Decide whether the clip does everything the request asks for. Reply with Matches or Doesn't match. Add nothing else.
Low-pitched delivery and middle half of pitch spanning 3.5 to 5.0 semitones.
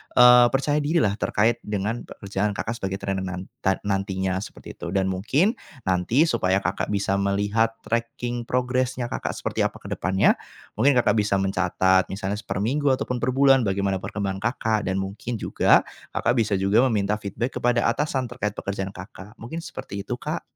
Matches